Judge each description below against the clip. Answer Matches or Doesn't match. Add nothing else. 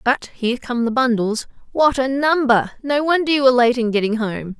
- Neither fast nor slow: Doesn't match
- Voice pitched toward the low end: Doesn't match